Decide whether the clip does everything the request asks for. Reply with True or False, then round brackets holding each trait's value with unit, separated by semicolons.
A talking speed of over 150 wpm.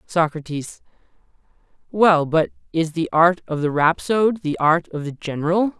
False (145 wpm)